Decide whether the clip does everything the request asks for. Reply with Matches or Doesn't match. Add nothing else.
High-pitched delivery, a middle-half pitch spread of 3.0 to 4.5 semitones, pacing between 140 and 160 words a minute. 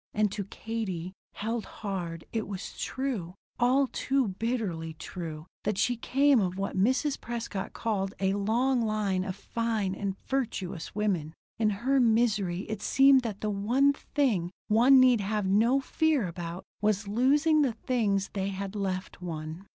Matches